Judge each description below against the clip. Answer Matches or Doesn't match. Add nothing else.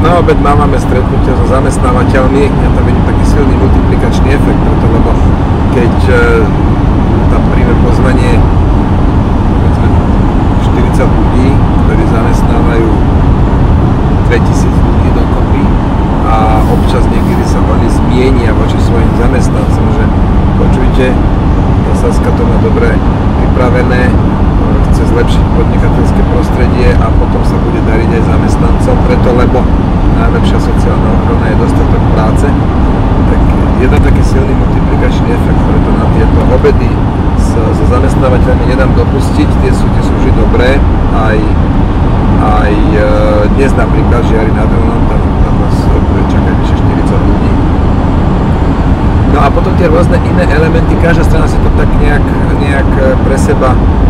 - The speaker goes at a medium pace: Matches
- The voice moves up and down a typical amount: Doesn't match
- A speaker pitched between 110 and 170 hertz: Doesn't match